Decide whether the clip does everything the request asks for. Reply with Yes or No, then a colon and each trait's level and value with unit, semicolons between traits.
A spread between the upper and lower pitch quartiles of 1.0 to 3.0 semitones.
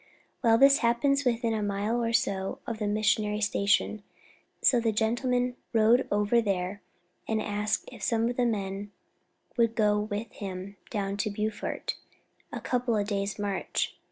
Yes: narrow, 2.4 semitones